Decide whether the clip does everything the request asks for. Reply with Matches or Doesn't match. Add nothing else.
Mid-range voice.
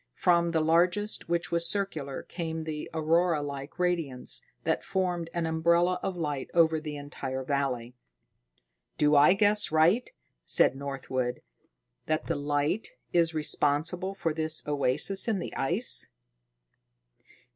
Matches